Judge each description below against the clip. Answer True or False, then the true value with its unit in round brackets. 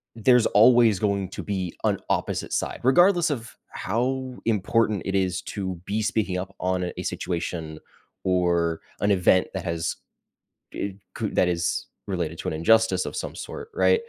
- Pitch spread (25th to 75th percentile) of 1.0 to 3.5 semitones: False (4.1 semitones)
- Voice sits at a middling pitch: False (95 Hz)